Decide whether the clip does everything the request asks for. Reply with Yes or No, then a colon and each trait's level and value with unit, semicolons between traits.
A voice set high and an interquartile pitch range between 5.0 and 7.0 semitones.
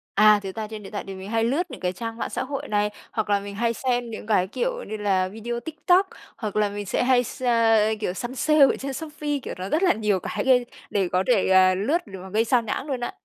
No: high, 225 Hz; average, 4.6 semitones